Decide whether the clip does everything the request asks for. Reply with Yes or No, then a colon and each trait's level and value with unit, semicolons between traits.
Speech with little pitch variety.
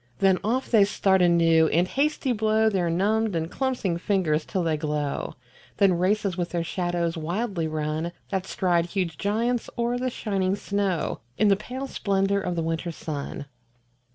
No: average, 4.1 semitones